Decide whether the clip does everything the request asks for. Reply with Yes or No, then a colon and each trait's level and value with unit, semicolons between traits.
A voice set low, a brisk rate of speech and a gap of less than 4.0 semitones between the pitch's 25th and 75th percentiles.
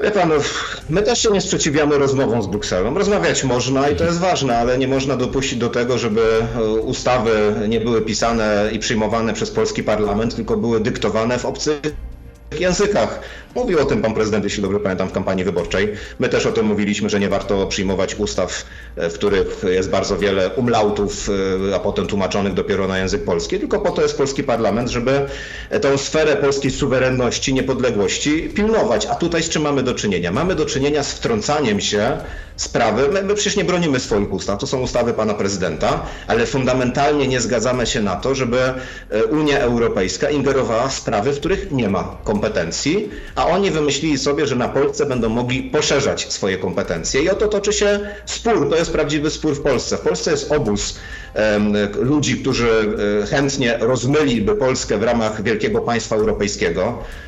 No: low, 130 Hz; fast, 175 wpm; average, 5.3 semitones